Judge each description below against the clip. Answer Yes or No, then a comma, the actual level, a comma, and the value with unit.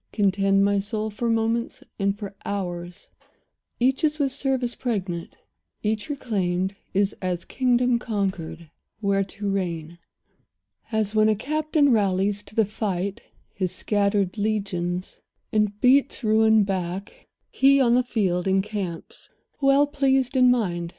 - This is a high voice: Yes, high, 205 Hz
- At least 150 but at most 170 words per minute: No, slow, 135 wpm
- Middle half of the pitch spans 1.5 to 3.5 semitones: No, average, 3.9 semitones